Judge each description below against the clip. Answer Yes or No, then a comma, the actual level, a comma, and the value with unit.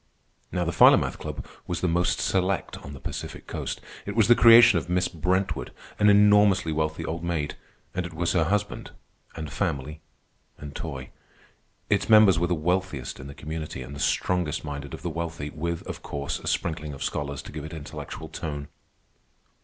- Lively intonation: No, average, 3.7 semitones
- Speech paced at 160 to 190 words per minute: Yes, average, 185 wpm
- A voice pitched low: Yes, very low, 80 Hz